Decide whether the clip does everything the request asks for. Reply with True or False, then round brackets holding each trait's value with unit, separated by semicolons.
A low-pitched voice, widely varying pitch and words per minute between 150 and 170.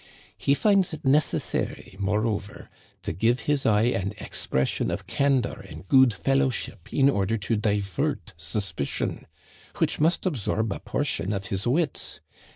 True (110 Hz; 5.8 semitones; 155 wpm)